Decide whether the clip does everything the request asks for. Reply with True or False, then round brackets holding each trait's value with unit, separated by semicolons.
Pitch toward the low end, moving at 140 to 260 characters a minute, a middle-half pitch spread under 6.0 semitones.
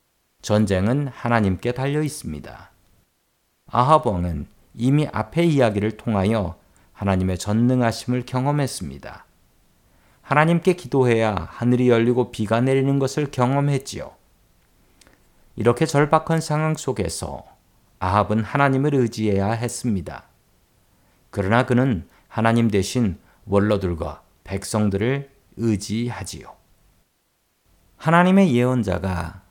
True (115 Hz; 255 characters per minute; 5.4 semitones)